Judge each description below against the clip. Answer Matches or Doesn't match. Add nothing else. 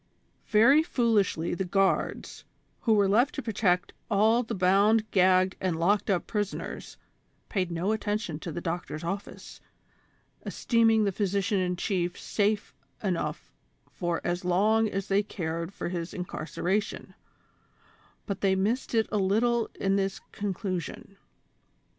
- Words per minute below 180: Matches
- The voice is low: Doesn't match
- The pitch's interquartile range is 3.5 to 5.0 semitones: Doesn't match